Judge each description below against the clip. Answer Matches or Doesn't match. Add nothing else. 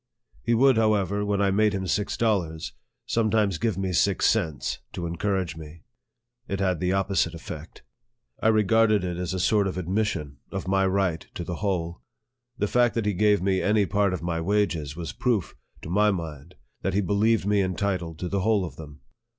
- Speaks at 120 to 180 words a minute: Doesn't match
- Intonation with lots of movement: Doesn't match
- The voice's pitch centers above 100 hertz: Doesn't match